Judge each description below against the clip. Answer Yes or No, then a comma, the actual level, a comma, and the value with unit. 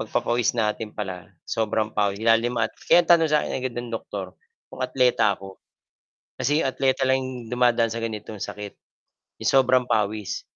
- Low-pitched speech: Yes, low, 115 Hz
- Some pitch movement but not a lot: Yes, average, 3.3 semitones